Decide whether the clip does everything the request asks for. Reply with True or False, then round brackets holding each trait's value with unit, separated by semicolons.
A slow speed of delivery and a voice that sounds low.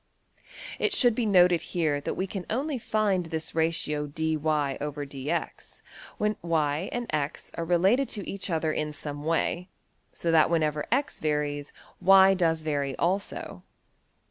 False (120 wpm; 165 Hz)